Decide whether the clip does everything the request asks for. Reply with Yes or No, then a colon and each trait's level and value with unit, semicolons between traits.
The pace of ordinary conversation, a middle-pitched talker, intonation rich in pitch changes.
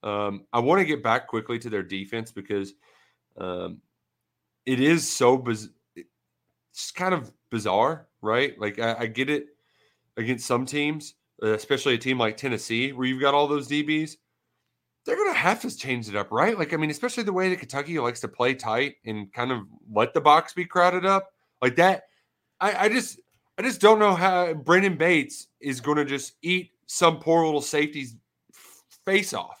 Yes: average, 190 wpm; medium, 145 Hz; wide, 7.1 semitones